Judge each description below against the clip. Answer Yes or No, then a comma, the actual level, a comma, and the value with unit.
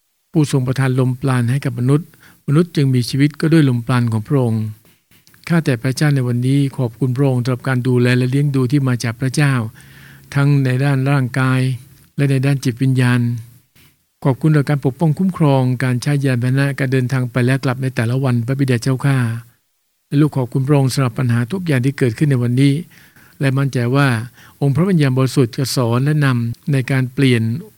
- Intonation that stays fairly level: Yes, narrow, 2.0 semitones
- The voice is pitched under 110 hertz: No, low, 135 Hz